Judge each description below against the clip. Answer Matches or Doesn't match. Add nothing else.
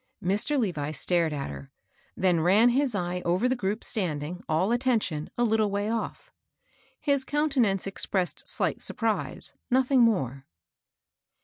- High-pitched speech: Matches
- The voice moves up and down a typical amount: Doesn't match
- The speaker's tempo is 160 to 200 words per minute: Doesn't match